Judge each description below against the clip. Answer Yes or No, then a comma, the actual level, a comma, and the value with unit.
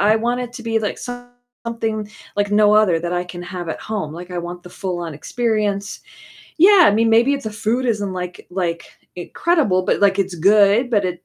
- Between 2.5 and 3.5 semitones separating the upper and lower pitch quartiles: No, average, 4.4 semitones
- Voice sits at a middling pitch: No, high, 205 Hz